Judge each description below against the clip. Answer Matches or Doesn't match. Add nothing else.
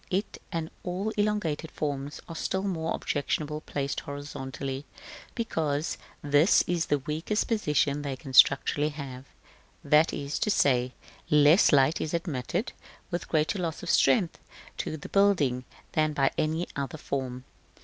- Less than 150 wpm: Matches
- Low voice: Doesn't match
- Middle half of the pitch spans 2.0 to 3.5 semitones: Matches